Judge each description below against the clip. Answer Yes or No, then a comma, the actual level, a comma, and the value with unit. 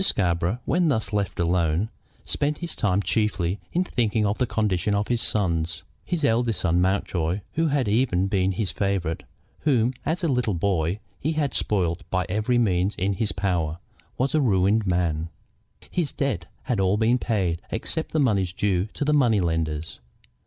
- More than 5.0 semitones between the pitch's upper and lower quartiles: Yes, wide, 5.5 semitones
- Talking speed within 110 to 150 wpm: No, average, 175 wpm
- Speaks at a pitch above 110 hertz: No, low, 100 Hz